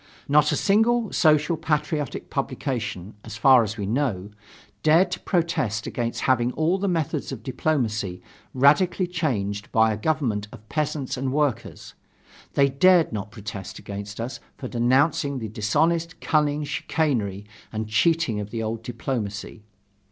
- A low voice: Yes, low, 130 Hz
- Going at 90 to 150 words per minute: Yes, average, 145 wpm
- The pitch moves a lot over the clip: Yes, wide, 6.2 semitones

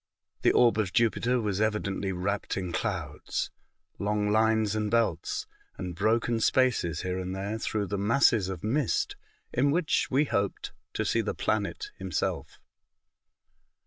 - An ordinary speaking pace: Yes, average, 145 wpm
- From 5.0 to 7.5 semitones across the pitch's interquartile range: No, average, 3.2 semitones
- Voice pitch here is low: Yes, low, 105 Hz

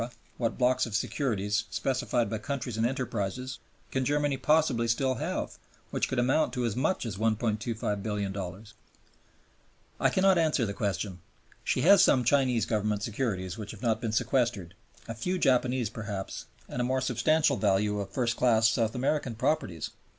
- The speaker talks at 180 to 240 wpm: No, average, 160 wpm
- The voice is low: Yes, low, 115 Hz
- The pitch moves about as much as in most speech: Yes, average, 3.7 semitones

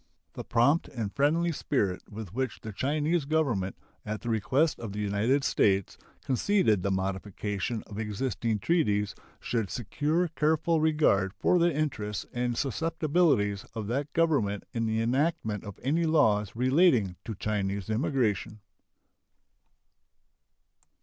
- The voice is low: Yes, low, 120 Hz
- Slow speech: Yes, slow, 130 wpm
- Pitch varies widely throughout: Yes, wide, 6.6 semitones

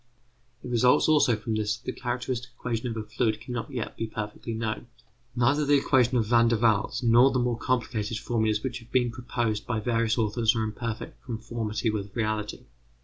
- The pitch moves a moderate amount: No, narrow, 2.1 semitones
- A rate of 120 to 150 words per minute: No, average, 200 wpm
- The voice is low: Yes, low, 115 Hz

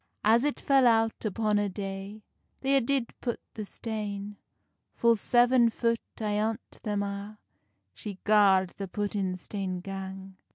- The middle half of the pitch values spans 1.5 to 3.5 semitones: Yes, average, 2.7 semitones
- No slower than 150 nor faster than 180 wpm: No, average, 140 wpm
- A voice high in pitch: Yes, high, 210 Hz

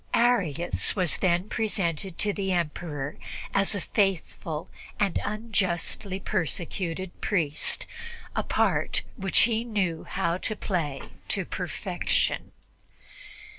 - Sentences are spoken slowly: Yes, slow, 105 wpm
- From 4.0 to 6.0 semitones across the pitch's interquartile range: No, average, 3.5 semitones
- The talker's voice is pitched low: No, medium, 185 Hz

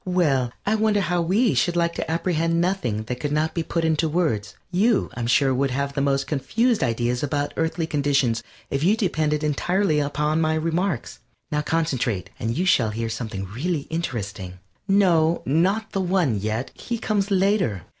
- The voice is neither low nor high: Yes, medium, 155 Hz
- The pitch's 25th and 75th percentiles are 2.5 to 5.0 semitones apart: No, wide, 5.6 semitones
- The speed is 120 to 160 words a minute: No, average, 175 wpm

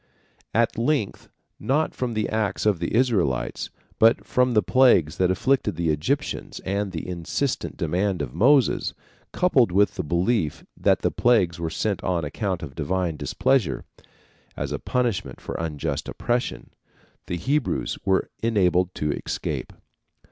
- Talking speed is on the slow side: No, average, 145 wpm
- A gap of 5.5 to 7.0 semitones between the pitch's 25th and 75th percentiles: Yes, wide, 6.1 semitones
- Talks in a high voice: No, low, 100 Hz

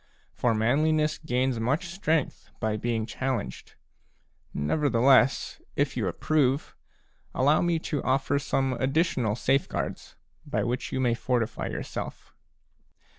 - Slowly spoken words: Yes, slow, 115 wpm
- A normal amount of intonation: Yes, average, 4.1 semitones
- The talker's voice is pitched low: Yes, low, 130 Hz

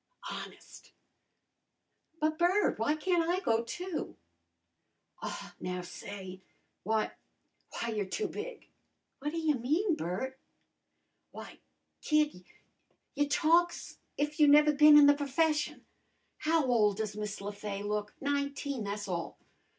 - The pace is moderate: No, slow, 125 wpm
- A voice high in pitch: Yes, very high, 280 Hz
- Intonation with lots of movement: Yes, wide, 6.7 semitones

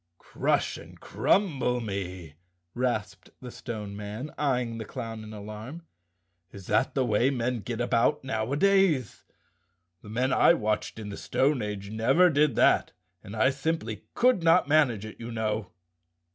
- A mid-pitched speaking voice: No, low, 120 Hz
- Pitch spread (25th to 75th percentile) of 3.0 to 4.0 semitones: No, average, 4.6 semitones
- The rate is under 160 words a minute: Yes, average, 150 wpm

